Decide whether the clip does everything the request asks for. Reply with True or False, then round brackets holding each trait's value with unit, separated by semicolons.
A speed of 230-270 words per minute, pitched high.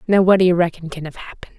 False (265 wpm; 175 Hz)